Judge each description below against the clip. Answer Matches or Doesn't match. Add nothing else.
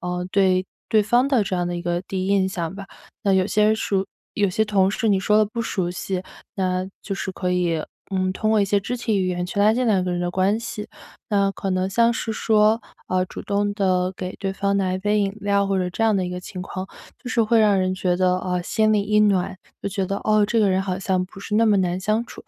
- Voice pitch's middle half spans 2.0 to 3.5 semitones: Matches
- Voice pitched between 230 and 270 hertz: Doesn't match